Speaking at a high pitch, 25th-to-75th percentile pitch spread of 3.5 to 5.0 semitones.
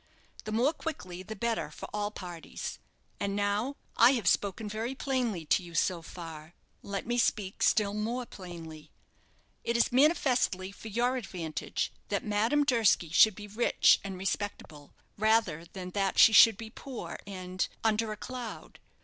Yes: high, 210 Hz; average, 4.2 semitones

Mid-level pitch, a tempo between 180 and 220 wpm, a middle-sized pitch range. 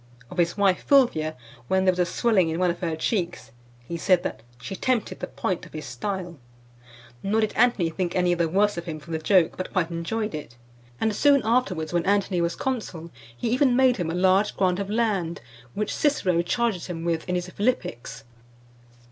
Yes: medium, 180 Hz; average, 200 wpm; average, 4.0 semitones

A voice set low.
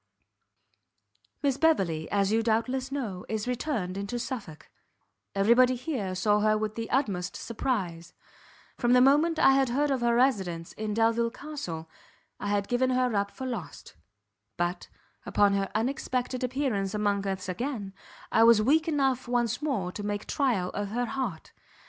No: high, 230 Hz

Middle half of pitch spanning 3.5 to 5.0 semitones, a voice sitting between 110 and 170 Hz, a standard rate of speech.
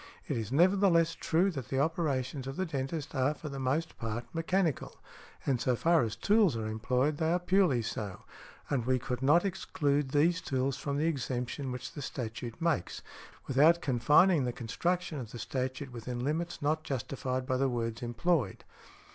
Yes: average, 4.7 semitones; low, 135 Hz; average, 175 wpm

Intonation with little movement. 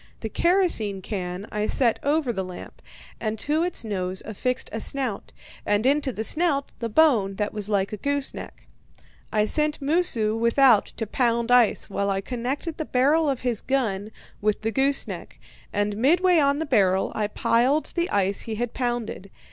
No: average, 5.2 semitones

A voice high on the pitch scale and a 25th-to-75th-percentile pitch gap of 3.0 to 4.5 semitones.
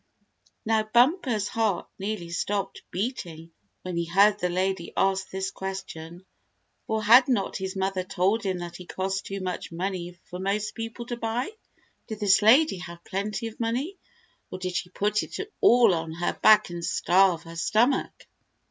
Yes: high, 195 Hz; average, 3.5 semitones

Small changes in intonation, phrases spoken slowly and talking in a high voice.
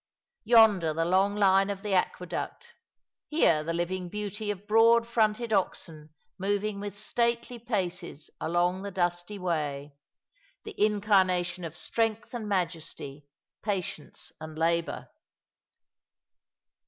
No: average, 3.7 semitones; slow, 115 wpm; high, 195 Hz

